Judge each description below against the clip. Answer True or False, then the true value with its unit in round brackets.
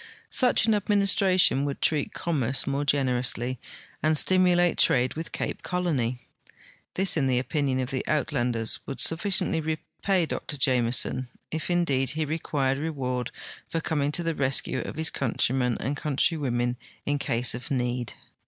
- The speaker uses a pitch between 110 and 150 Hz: True (140 Hz)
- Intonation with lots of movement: False (4.3 semitones)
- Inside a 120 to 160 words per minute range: True (150 wpm)